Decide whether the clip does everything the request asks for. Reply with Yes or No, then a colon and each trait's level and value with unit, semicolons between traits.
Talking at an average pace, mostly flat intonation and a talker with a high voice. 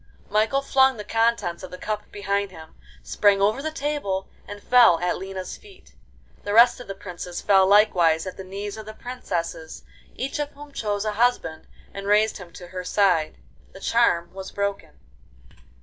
No: average, 180 wpm; average, 3.9 semitones; high, 205 Hz